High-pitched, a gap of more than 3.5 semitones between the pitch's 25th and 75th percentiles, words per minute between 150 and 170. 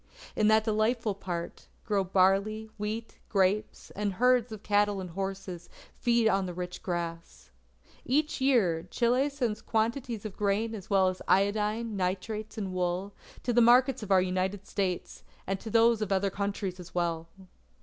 No: high, 205 Hz; average, 3.1 semitones; average, 165 wpm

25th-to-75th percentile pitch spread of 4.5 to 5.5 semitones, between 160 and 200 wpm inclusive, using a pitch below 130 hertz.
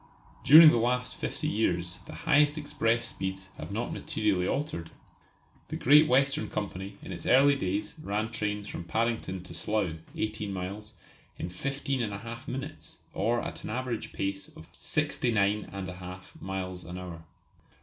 No: average, 5.2 semitones; average, 150 wpm; low, 105 Hz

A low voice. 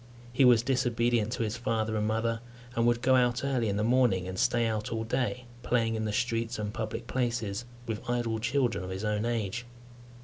Yes: low, 115 Hz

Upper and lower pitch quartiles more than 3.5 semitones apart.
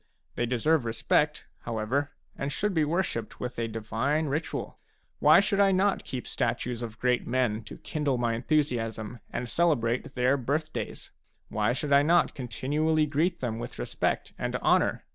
Yes: average, 4.7 semitones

